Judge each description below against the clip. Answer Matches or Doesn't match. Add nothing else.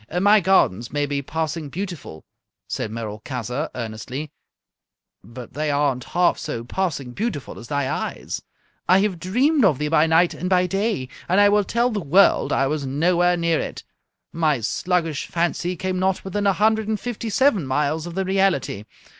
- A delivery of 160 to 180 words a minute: Matches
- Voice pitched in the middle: Matches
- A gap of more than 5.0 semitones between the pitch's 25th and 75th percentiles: Matches